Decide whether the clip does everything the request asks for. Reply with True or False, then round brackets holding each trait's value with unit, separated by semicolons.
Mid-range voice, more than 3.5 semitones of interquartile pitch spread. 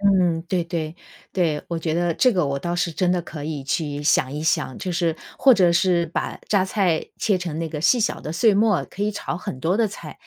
False (170 Hz; 3.2 semitones)